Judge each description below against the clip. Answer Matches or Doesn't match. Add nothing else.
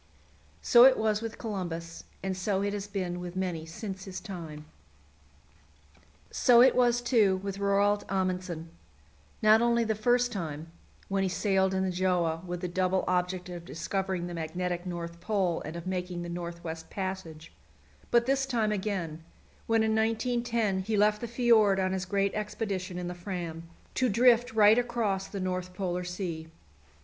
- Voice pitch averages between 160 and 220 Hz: Matches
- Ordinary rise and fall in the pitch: Matches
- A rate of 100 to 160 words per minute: Doesn't match